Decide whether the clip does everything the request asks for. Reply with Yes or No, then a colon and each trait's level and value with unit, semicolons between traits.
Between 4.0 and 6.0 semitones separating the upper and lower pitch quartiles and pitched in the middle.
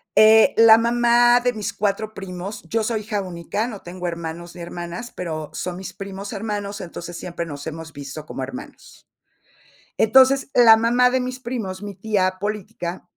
No: average, 4.6 semitones; high, 200 Hz